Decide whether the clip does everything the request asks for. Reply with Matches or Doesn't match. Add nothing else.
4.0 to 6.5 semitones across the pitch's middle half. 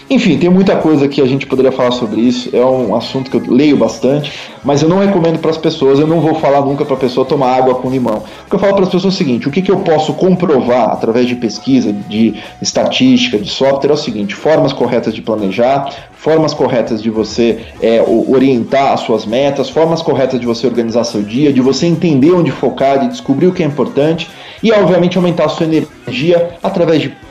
Matches